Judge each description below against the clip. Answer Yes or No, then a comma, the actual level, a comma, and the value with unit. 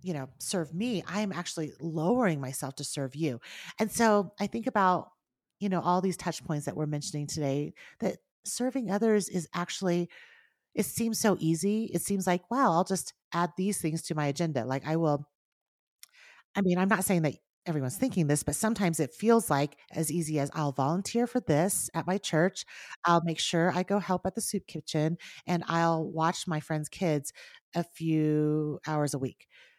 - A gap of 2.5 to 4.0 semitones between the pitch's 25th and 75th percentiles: No, average, 4.5 semitones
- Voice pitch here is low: No, medium, 170 Hz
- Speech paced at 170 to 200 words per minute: Yes, average, 195 wpm